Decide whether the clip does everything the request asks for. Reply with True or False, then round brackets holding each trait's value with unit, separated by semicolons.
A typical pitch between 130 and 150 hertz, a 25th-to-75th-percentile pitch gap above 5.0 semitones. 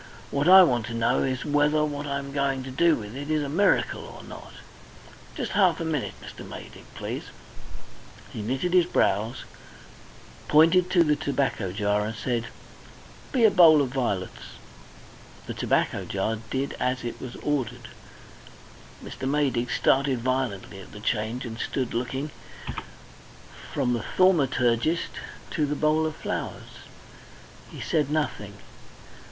False (135 Hz; 4.3 semitones)